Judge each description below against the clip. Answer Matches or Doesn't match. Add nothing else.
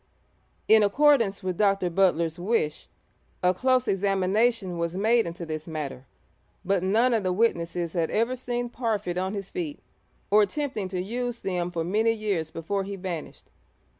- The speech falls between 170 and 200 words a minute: Doesn't match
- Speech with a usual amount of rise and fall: Matches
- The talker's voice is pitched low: Doesn't match